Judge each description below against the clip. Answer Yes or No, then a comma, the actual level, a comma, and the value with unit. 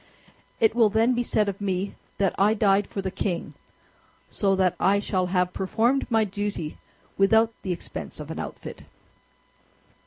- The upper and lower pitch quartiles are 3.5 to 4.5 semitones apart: No, average, 2.8 semitones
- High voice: Yes, high, 200 Hz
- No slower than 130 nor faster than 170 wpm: Yes, average, 160 wpm